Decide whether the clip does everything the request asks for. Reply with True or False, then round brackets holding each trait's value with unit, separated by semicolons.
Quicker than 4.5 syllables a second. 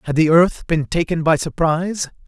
True (5.1 syllables/s)